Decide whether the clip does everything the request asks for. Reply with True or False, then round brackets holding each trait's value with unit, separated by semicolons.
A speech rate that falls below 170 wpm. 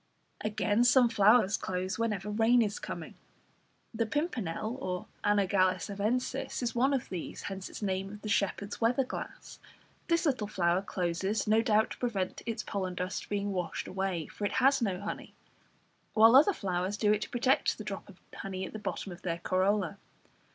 False (175 wpm)